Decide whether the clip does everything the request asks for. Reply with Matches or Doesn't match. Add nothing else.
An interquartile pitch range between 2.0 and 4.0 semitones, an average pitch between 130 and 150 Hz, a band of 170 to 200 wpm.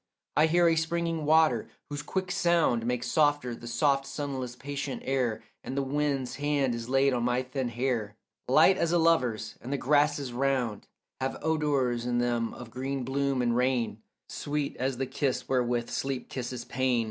Matches